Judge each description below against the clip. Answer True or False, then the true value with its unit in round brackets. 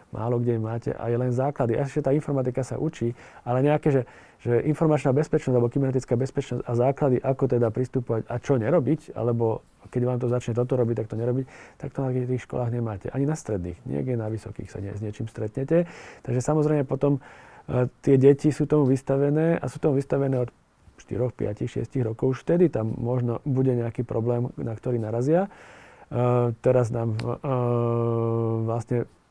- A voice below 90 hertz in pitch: False (125 Hz)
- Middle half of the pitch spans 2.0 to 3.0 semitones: True (2.7 semitones)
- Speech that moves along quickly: True (180 wpm)